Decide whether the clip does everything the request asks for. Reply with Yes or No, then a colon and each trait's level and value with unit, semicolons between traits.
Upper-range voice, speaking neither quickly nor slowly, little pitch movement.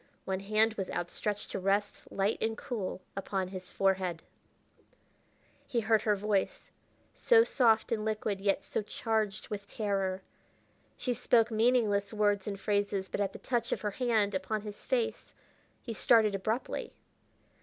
Yes: high, 210 Hz; average, 150 wpm; narrow, 2.2 semitones